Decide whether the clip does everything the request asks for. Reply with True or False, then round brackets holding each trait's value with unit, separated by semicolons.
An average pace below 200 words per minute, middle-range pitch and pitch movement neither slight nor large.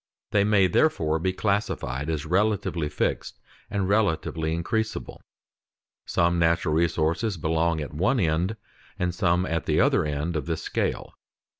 False (140 wpm; 85 Hz; 3.9 semitones)